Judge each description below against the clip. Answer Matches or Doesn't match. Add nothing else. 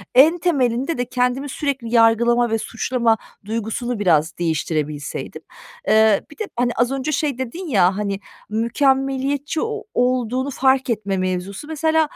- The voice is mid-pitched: Doesn't match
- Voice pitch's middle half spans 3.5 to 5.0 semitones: Matches